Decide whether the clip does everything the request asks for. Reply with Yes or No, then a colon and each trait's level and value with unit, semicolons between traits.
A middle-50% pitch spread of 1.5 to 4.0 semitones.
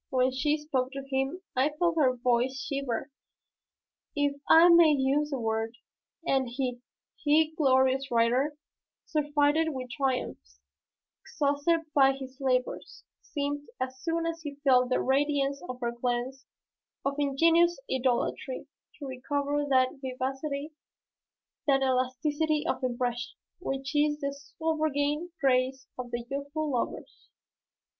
Yes: narrow, 2.5 semitones